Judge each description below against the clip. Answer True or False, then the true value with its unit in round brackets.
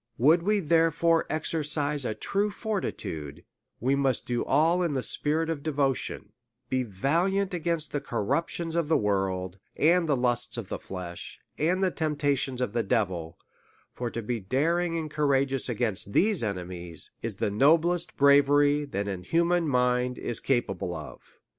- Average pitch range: False (6.2 semitones)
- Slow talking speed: False (160 wpm)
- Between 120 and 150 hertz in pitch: True (140 Hz)